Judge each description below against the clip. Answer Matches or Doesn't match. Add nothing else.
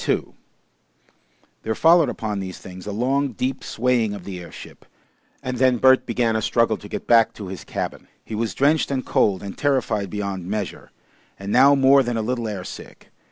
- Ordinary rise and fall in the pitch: Matches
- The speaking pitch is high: Doesn't match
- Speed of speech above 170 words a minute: Matches